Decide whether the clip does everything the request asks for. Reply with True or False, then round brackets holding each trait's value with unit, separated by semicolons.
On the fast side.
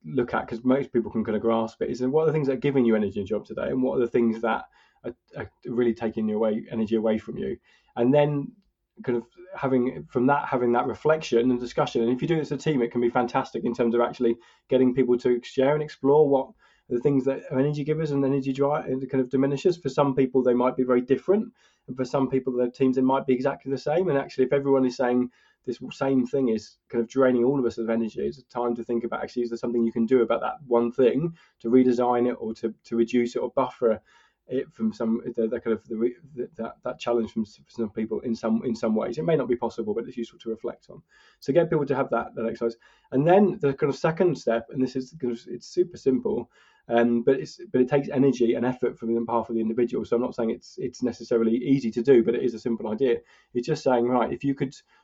True (265 wpm)